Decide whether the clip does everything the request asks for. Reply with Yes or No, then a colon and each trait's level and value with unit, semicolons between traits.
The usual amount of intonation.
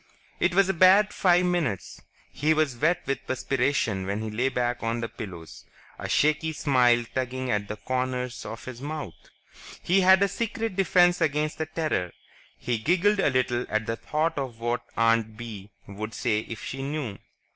No: wide, 5.8 semitones